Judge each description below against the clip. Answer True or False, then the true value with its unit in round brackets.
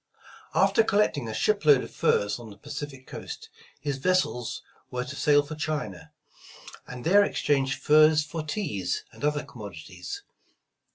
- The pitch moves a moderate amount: True (4.3 semitones)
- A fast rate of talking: False (155 wpm)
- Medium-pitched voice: True (145 Hz)